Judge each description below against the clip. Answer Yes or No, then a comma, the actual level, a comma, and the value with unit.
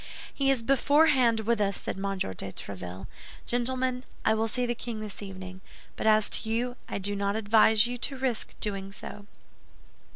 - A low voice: No, high, 220 Hz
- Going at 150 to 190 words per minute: Yes, average, 185 wpm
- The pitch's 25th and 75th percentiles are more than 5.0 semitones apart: No, average, 3.7 semitones